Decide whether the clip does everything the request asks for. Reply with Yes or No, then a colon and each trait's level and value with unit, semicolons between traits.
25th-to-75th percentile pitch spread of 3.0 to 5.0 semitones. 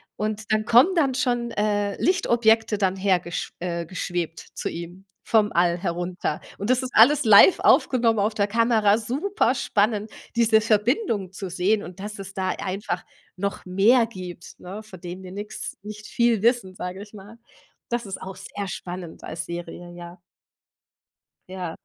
Yes: average, 3.7 semitones